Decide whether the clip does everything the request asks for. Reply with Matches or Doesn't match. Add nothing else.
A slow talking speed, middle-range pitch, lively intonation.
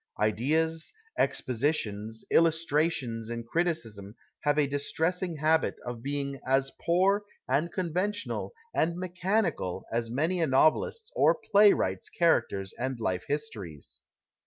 Matches